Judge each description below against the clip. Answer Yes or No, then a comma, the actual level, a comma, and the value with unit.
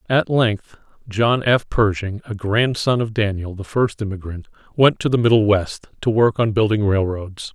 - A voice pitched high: No, low, 110 Hz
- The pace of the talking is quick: No, average, 175 wpm